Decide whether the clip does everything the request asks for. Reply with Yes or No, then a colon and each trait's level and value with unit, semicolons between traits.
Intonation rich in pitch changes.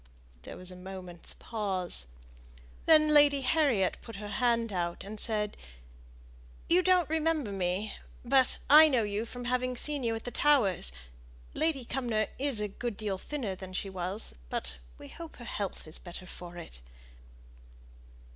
Yes: wide, 6.3 semitones